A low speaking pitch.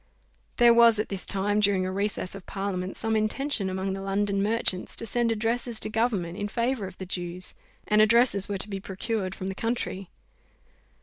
No: high, 205 Hz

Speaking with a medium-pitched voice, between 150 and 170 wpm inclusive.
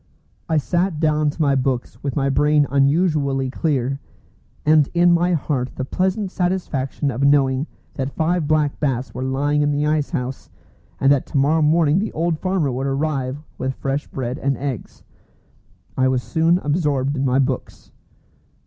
Yes: medium, 145 Hz; average, 165 wpm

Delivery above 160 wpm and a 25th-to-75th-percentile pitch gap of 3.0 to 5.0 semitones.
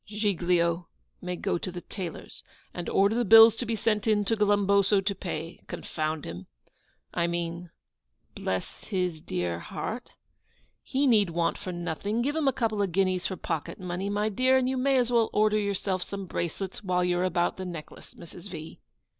Yes: average, 180 wpm; average, 3.7 semitones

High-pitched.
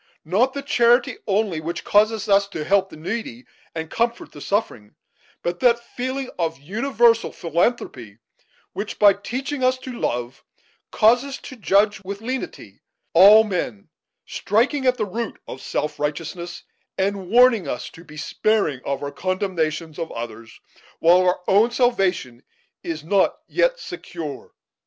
Yes: high, 200 Hz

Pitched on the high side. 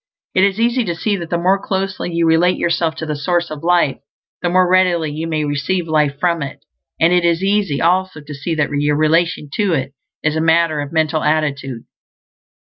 No: medium, 165 Hz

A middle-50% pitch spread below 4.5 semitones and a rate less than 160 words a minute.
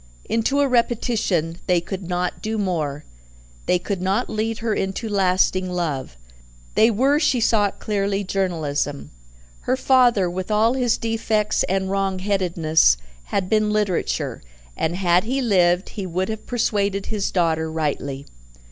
Yes: average, 3.8 semitones; average, 145 wpm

